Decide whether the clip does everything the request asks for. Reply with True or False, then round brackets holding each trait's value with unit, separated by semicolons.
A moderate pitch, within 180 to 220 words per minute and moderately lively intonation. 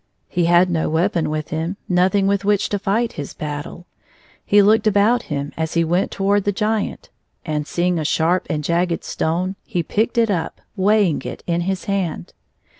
True (180 Hz; 185 wpm; 3.8 semitones)